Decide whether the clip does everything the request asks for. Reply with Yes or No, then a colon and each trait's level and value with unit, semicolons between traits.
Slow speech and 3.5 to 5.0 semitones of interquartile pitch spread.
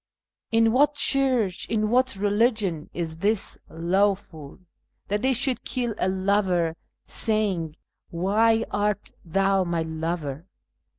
Yes: slow, 120 wpm; average, 4.7 semitones